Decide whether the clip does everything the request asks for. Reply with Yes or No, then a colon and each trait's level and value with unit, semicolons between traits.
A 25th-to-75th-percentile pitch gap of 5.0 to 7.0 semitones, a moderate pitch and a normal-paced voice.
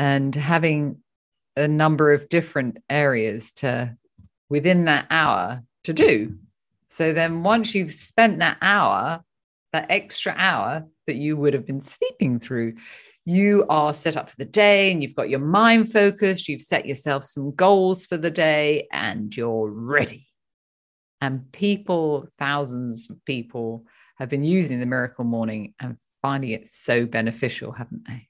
Yes: wide, 5.6 semitones; medium, 145 Hz; average, 155 wpm